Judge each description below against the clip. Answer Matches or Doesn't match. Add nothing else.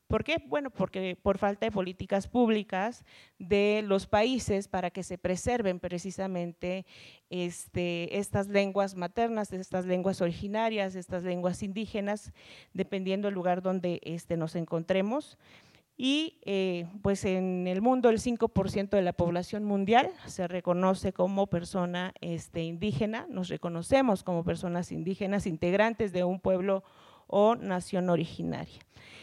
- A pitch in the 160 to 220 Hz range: Matches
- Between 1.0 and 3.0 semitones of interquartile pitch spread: Matches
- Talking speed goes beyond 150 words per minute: Doesn't match